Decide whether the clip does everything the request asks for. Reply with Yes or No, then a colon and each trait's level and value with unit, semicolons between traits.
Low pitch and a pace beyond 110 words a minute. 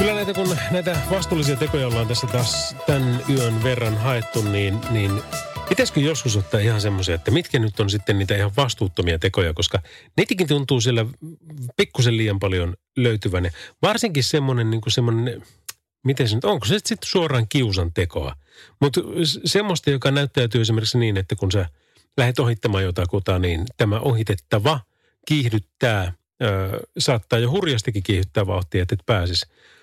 Yes: low, 115 Hz; fast, 155 wpm